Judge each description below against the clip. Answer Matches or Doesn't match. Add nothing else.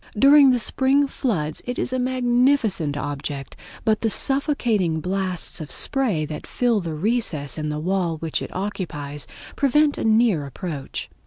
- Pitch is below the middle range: Doesn't match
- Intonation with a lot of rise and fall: Matches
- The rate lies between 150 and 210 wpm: Matches